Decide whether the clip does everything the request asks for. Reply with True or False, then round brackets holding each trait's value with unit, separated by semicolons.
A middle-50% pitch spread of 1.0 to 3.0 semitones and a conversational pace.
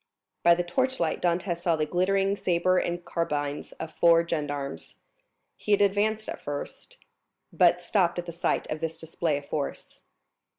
True (2.5 semitones; 160 wpm)